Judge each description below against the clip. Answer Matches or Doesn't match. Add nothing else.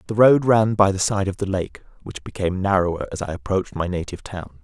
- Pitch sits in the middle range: Doesn't match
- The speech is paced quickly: Matches